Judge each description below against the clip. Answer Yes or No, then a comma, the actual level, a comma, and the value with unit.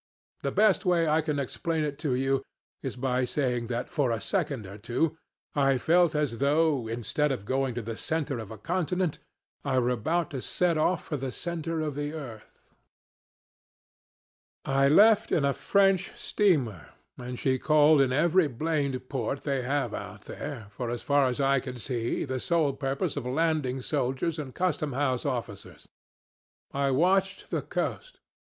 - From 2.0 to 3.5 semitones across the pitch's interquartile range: No, average, 4.0 semitones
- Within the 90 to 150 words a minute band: No, average, 170 wpm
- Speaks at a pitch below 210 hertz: Yes, medium, 140 Hz